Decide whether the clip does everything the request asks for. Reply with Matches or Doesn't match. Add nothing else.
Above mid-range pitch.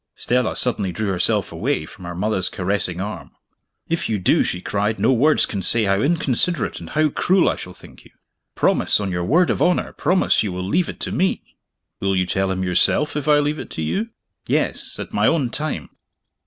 Doesn't match